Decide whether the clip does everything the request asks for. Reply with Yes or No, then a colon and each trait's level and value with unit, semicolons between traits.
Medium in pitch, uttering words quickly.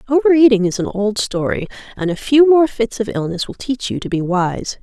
No: high, 225 Hz; fast, 225 wpm